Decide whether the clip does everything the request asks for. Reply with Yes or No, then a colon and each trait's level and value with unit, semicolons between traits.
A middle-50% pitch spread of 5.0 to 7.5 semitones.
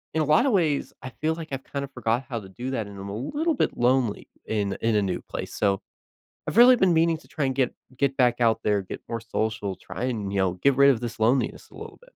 Yes: average, 5.3 semitones